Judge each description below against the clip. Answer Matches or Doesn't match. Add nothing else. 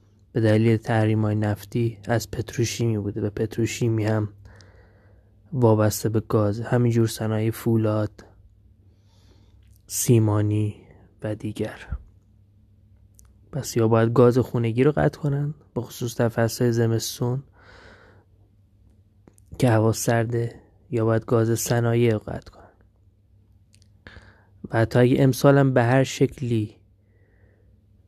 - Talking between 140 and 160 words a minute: Doesn't match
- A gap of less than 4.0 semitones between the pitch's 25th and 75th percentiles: Matches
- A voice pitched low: Matches